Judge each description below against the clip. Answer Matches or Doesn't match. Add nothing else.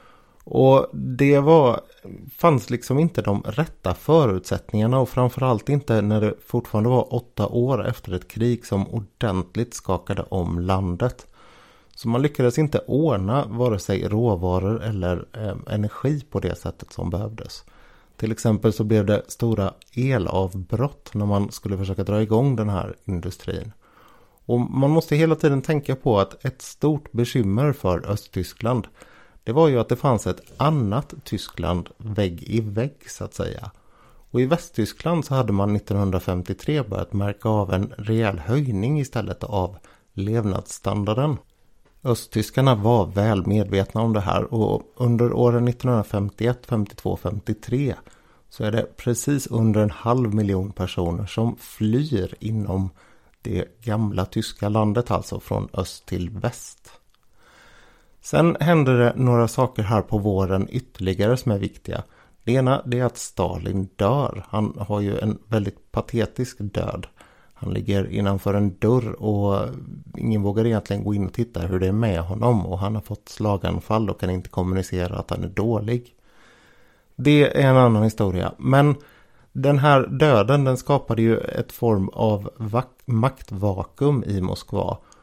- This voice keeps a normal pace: Matches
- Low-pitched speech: Matches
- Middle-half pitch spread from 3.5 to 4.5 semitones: Matches